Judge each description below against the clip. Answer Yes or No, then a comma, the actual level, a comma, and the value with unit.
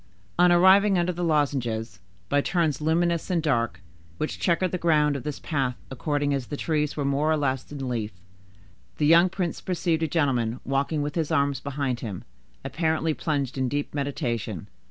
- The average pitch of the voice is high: No, medium, 145 Hz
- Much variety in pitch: No, average, 3.7 semitones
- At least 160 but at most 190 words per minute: Yes, average, 180 wpm